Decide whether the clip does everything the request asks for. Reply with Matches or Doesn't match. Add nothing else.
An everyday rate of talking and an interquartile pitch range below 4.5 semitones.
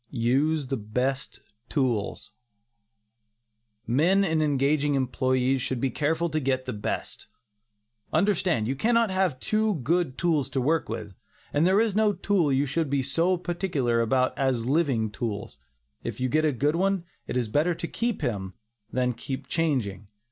Doesn't match